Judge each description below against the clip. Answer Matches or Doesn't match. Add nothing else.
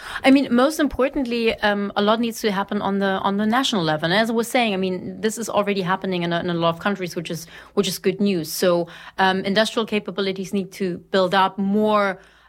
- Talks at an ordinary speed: Doesn't match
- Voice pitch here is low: Doesn't match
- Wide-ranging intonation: Doesn't match